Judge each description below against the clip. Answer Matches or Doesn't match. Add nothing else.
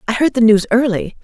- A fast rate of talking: Matches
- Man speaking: Doesn't match